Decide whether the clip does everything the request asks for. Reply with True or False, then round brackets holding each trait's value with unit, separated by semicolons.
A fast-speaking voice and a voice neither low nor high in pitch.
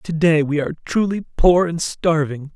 False (165 wpm; 160 Hz)